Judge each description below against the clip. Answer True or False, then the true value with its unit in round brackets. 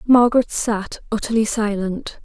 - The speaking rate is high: False (105 wpm)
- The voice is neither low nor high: False (220 Hz)